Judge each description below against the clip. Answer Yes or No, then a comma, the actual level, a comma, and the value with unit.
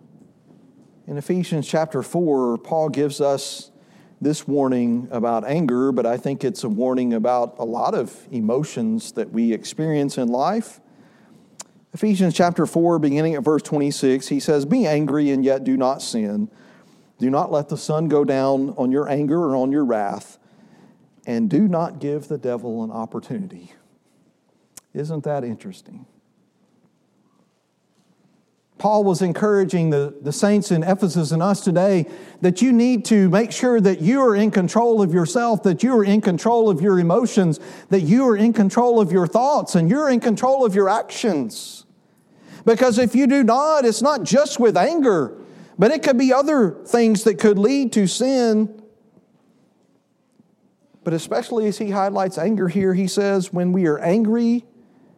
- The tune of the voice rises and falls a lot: Yes, wide, 7.1 semitones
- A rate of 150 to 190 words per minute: Yes, average, 160 wpm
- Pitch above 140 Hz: Yes, high, 190 Hz